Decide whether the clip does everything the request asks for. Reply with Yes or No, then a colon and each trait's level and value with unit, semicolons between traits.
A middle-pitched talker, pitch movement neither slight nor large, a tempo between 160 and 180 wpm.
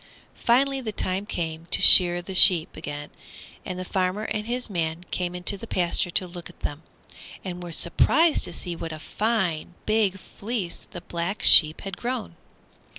Yes: medium, 180 Hz; average, 3.7 semitones; average, 175 wpm